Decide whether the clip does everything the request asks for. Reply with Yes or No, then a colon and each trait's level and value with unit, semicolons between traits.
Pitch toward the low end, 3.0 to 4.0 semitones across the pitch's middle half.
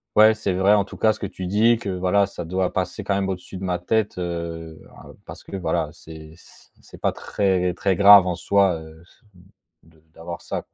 No: very low, 95 Hz; narrow, 2.6 semitones